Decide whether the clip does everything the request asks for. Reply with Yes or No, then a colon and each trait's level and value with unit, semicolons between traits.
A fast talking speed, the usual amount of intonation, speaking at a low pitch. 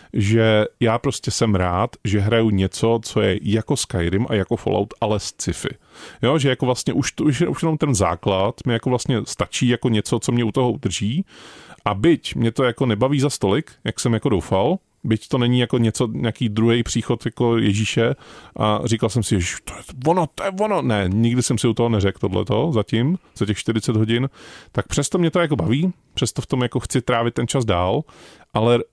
Yes: fast, 210 wpm; average, 3.1 semitones; low, 120 Hz